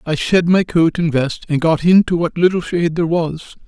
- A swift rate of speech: Yes, fast, 230 wpm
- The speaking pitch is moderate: Yes, medium, 165 Hz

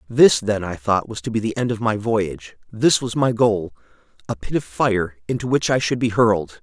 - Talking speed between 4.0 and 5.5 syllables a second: Yes, 5.1 syllables/s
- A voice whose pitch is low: Yes, low, 115 Hz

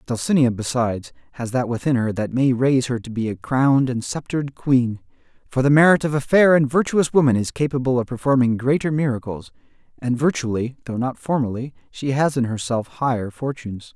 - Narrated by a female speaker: No, male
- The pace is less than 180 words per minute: No, average, 185 wpm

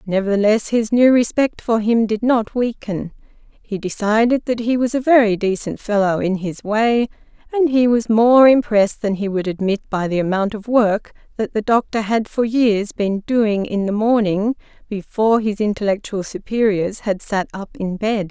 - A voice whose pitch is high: Yes, high, 215 Hz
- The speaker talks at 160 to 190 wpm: Yes, average, 180 wpm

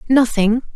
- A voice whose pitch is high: Yes, high, 235 Hz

